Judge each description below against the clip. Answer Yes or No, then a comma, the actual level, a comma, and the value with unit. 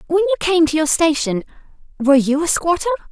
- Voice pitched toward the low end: No, very high, 300 Hz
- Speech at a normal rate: Yes, average, 195 wpm